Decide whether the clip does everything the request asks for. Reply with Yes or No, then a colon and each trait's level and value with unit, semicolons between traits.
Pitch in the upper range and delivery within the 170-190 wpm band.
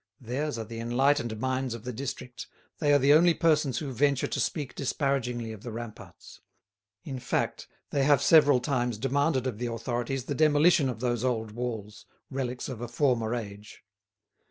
No: low, 125 Hz; average, 175 wpm